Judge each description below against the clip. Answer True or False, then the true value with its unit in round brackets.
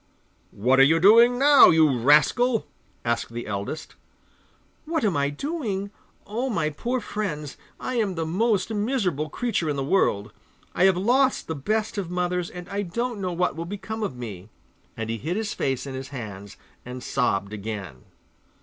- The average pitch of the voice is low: False (175 Hz)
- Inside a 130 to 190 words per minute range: True (175 wpm)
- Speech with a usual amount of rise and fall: False (8.3 semitones)